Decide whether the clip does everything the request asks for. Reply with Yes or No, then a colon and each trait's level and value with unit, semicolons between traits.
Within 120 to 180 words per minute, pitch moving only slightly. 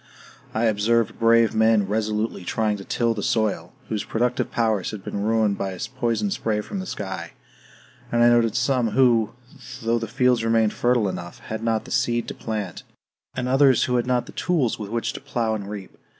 No: average, 195 wpm; narrow, 2.1 semitones